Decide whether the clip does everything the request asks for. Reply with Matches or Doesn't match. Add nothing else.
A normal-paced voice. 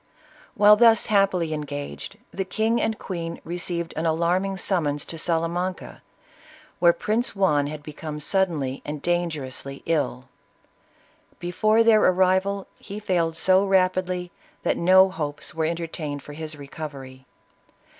Doesn't match